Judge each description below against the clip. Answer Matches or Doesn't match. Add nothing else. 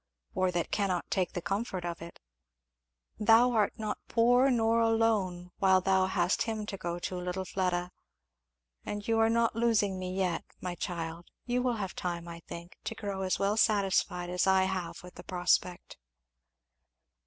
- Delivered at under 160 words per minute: Doesn't match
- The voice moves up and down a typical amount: Matches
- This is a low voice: Doesn't match